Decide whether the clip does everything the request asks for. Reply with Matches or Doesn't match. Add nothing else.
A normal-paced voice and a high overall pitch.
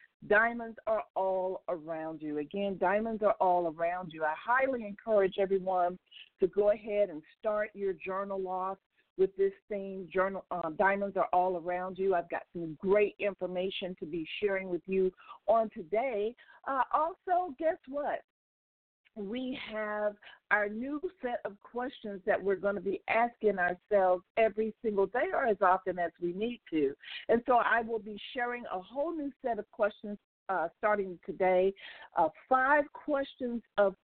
Matches